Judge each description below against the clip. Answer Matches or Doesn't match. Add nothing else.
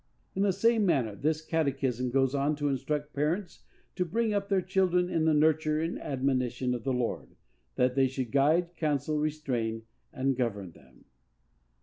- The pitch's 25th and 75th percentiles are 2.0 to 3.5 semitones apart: Doesn't match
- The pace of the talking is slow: Doesn't match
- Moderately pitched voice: Matches